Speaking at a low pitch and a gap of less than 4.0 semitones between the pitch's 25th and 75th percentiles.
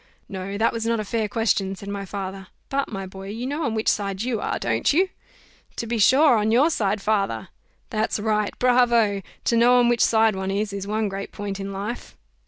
No: high, 215 Hz; average, 2.9 semitones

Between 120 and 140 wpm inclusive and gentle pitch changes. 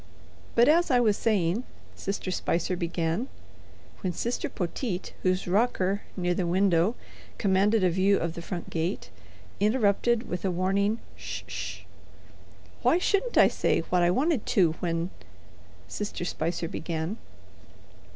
No: slow, 135 wpm; average, 4.0 semitones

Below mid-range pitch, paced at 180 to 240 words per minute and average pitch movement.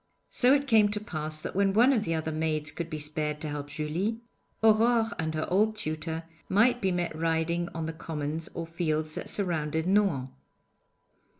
No: medium, 165 Hz; average, 185 wpm; average, 4.9 semitones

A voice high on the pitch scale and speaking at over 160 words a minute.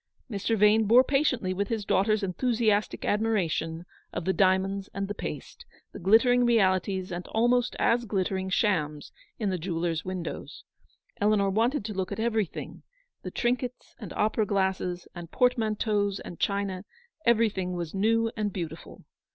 No: high, 200 Hz; average, 150 wpm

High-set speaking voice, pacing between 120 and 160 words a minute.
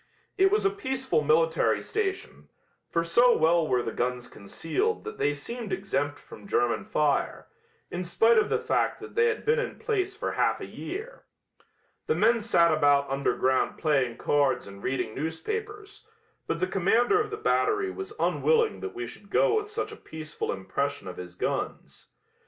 No: high, 195 Hz; average, 175 wpm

